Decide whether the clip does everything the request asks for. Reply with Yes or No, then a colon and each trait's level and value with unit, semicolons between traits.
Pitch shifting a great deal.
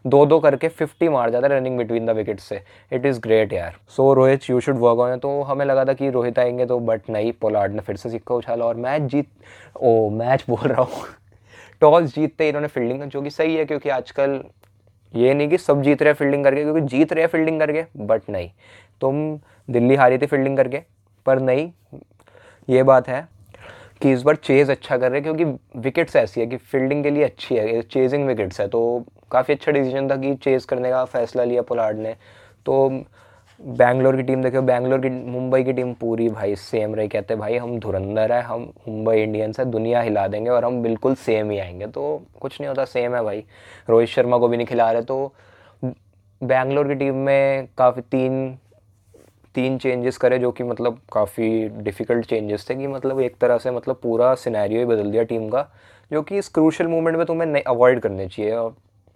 No: average, 3.3 semitones